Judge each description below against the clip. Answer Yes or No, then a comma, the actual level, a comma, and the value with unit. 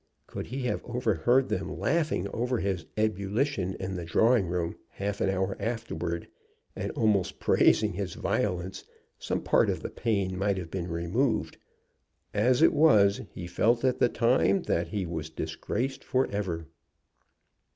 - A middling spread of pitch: Yes, average, 5.0 semitones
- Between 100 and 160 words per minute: Yes, average, 150 wpm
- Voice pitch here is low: Yes, low, 100 Hz